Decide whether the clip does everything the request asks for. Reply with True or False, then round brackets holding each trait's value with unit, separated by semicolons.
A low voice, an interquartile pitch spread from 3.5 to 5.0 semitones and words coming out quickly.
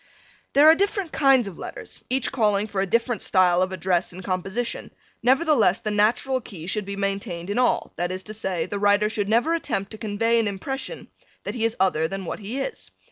False (210 Hz; 4.3 semitones; 210 wpm)